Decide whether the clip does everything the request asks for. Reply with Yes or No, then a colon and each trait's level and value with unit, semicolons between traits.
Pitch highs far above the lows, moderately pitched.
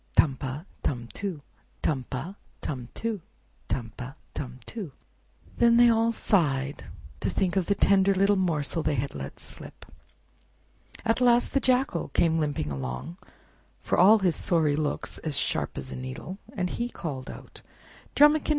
Yes: wide, 7.1 semitones; medium, 165 Hz